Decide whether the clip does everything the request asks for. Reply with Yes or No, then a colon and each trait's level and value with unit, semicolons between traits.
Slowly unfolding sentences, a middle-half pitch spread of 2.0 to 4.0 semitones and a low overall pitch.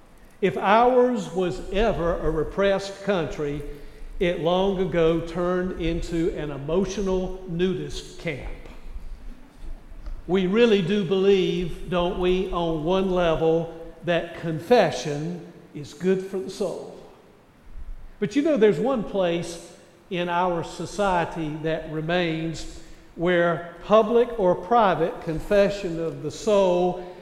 No: slow, 110 wpm; average, 2.7 semitones; medium, 180 Hz